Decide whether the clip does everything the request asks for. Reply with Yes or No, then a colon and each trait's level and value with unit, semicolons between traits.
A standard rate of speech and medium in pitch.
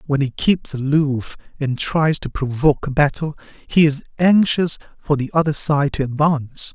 Yes: average, 170 wpm; medium, 145 Hz